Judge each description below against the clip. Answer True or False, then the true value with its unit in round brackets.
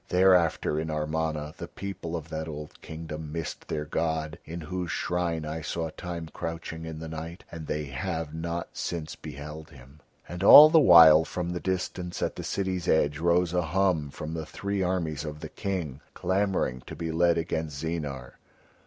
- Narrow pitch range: True (2.3 semitones)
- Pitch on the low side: True (80 Hz)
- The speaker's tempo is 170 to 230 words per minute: True (180 wpm)